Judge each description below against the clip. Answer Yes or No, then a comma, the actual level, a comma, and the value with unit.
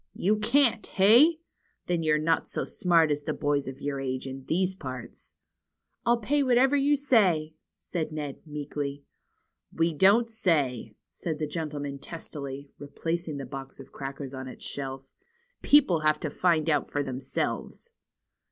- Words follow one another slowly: No, average, 160 wpm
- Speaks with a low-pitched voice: No, medium, 155 Hz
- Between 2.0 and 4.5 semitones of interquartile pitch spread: No, wide, 5.4 semitones